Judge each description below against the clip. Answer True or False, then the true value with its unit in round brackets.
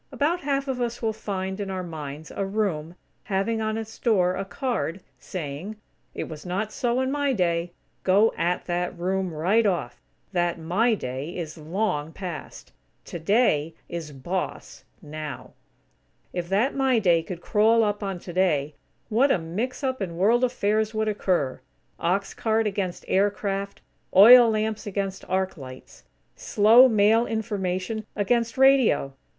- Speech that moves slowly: False (150 wpm)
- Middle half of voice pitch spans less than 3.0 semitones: False (4.3 semitones)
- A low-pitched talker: False (195 Hz)